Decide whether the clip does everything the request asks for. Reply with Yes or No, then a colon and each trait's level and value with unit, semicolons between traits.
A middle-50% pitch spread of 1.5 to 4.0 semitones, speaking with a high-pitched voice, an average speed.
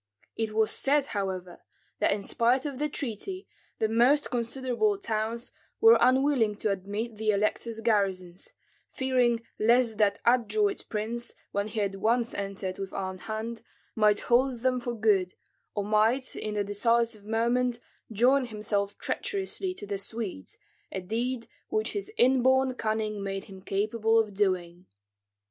Yes: average, 3.5 semitones; high, 225 Hz; average, 145 wpm